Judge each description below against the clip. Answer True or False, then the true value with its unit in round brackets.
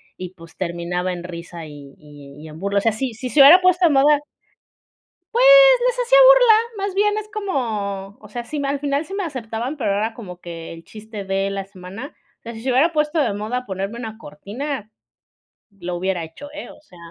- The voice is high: True (220 Hz)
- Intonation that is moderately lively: False (8.1 semitones)